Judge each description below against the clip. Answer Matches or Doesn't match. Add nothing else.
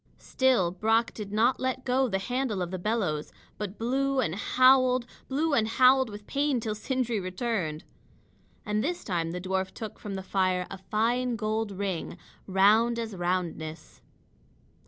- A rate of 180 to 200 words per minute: Doesn't match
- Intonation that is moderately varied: Matches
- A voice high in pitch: Matches